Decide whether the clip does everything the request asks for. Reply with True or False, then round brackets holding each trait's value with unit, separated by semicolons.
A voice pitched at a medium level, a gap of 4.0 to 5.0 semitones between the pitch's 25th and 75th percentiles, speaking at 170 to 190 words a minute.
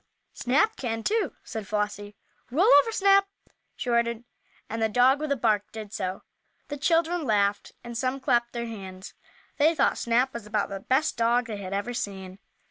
False (235 Hz; 4.6 semitones; 180 wpm)